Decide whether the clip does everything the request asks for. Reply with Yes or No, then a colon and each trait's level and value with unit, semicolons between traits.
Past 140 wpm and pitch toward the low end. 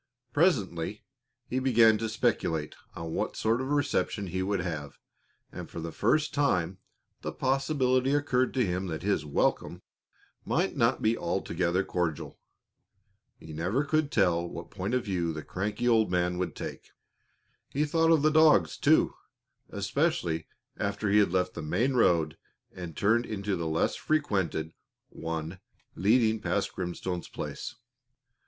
Yes: average, 150 wpm; low, 100 Hz